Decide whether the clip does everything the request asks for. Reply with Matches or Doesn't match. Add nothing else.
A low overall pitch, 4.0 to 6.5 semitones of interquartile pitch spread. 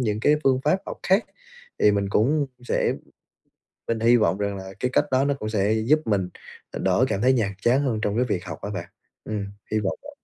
Matches